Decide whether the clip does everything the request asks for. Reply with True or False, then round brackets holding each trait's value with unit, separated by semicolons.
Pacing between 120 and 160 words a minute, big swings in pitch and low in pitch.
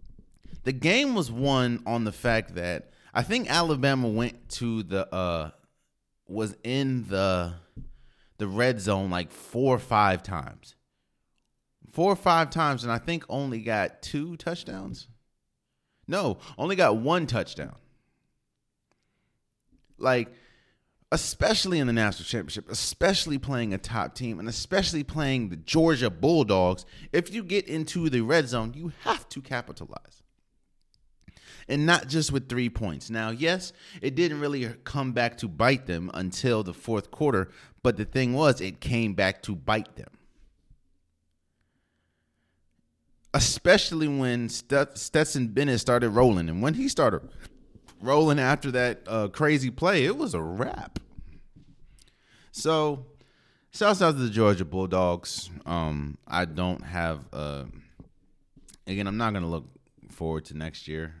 True (140 wpm; 7.2 semitones; 120 Hz)